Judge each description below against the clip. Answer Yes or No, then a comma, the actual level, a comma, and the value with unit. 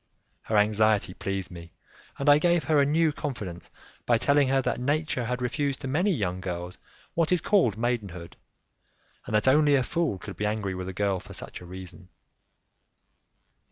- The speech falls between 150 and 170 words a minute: No, average, 180 wpm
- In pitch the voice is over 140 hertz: No, low, 115 Hz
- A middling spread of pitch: No, wide, 7.4 semitones